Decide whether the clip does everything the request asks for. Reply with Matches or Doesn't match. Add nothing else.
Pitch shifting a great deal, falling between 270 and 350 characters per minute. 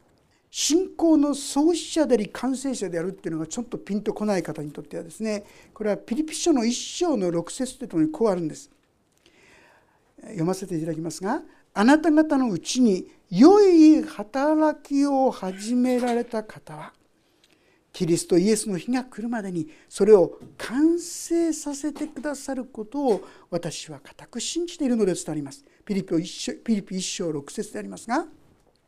Matches